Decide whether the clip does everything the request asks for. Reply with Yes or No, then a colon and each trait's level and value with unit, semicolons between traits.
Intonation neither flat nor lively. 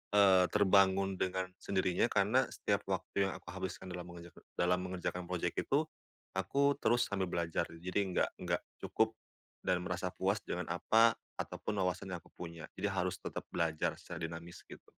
No: narrow, 2.0 semitones